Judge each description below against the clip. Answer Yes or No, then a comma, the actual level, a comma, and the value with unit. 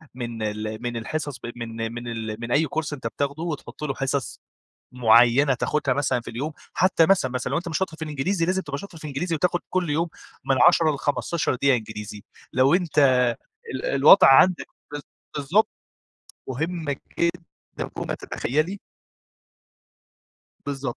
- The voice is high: No, medium, 140 Hz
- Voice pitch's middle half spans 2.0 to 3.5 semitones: No, average, 5.1 semitones